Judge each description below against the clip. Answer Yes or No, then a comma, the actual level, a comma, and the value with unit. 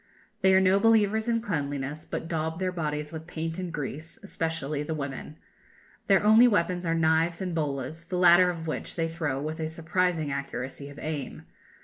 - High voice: No, medium, 165 Hz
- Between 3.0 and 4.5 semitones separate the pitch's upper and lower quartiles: Yes, average, 3.3 semitones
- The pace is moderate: Yes, average, 185 wpm